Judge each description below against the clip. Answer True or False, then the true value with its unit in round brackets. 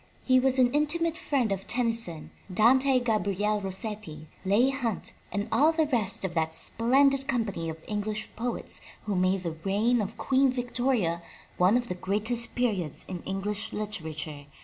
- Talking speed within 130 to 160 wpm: True (155 wpm)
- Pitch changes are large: False (4.8 semitones)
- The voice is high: True (215 Hz)